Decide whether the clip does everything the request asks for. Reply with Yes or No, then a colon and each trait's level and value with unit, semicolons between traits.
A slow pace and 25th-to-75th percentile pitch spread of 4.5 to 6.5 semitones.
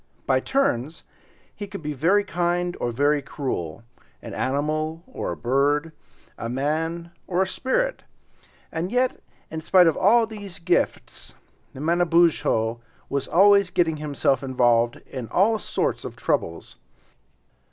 Yes: slow, 130 wpm; average, 5.2 semitones